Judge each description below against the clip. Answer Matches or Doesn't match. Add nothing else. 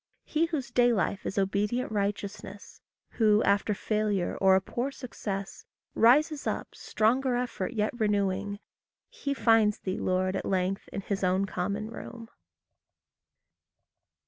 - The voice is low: Doesn't match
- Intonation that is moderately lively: Matches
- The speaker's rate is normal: Doesn't match